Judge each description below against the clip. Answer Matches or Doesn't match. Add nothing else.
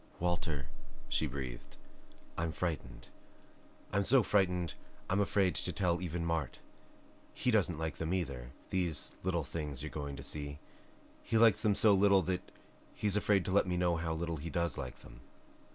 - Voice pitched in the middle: Doesn't match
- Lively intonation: Doesn't match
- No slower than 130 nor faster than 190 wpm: Matches